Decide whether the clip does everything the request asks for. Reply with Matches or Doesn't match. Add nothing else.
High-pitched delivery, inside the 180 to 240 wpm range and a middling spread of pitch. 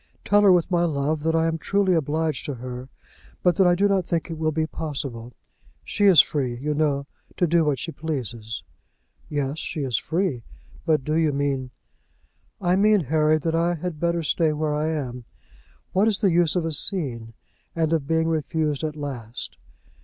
Doesn't match